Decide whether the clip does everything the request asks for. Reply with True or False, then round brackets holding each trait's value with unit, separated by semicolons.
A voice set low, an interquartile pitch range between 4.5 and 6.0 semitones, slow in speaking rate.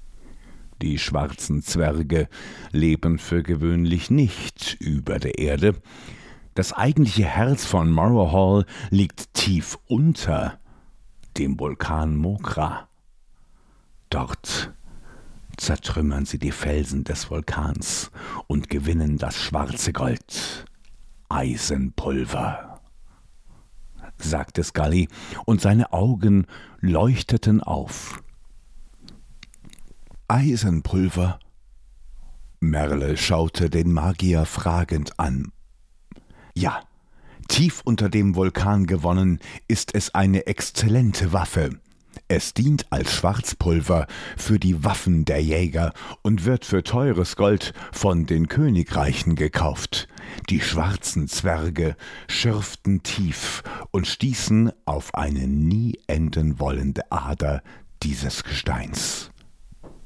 True (85 Hz; 5.1 semitones; 90 wpm)